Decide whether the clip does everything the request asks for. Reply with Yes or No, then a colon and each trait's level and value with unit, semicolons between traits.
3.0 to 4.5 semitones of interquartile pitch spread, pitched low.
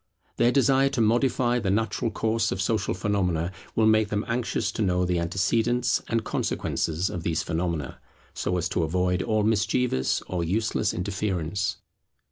Yes: average, 4.2 semitones; low, 105 Hz